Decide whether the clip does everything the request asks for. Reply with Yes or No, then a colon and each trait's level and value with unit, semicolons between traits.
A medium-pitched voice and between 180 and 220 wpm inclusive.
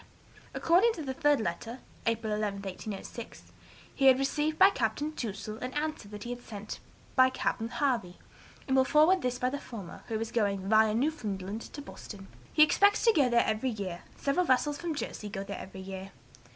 No: high, 235 Hz; average, 190 wpm